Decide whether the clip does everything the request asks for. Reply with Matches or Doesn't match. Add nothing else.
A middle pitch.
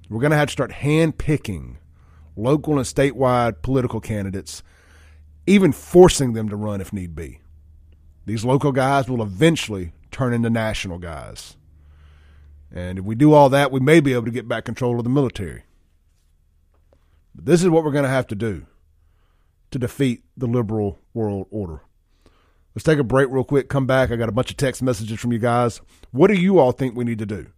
Doesn't match